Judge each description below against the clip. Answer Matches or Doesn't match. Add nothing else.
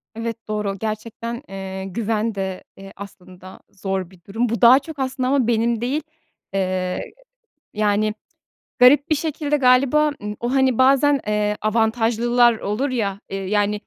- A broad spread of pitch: Doesn't match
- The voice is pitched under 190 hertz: Doesn't match